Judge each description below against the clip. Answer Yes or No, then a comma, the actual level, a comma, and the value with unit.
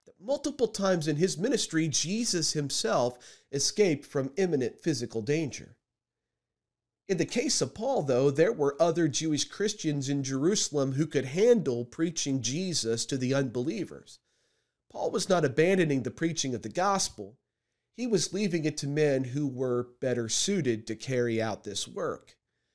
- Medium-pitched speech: Yes, medium, 145 Hz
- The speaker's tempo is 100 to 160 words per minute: Yes, average, 150 wpm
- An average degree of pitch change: No, wide, 5.9 semitones